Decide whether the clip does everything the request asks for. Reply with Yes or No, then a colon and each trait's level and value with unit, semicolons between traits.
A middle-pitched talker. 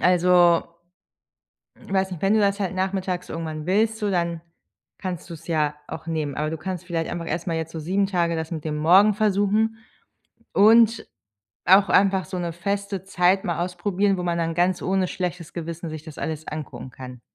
Yes: medium, 180 Hz